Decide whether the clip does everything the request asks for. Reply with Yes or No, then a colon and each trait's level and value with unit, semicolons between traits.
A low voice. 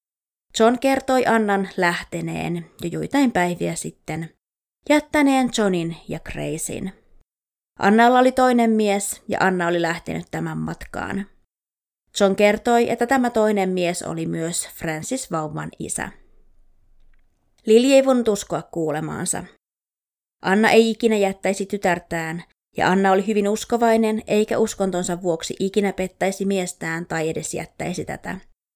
No: high, 195 Hz